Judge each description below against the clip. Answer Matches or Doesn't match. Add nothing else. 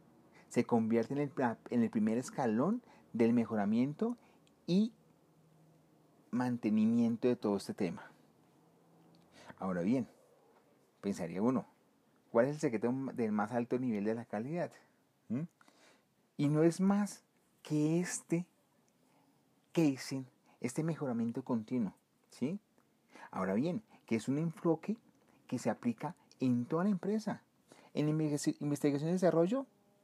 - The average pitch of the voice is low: Doesn't match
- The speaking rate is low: Matches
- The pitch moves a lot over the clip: Matches